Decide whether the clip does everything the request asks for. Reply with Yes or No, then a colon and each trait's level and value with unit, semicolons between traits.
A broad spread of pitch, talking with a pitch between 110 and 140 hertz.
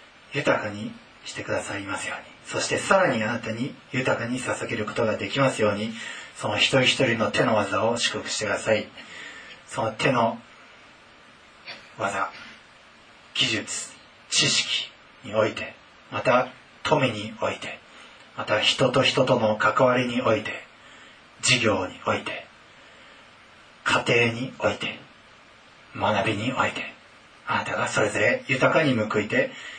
No: average, 3.2 semitones; low, 120 Hz